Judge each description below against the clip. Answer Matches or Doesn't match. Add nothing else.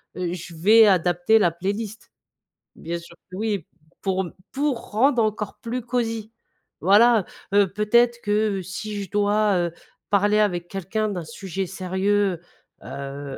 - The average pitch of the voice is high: Matches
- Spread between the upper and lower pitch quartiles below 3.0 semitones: Doesn't match